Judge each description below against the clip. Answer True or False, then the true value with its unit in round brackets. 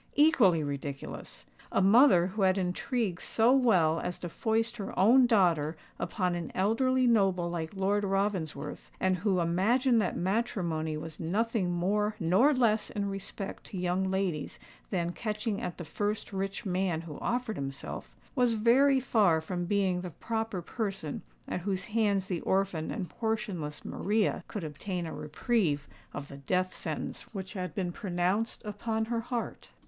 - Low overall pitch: False (195 Hz)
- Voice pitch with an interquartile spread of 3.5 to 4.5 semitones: True (4.2 semitones)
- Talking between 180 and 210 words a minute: False (155 wpm)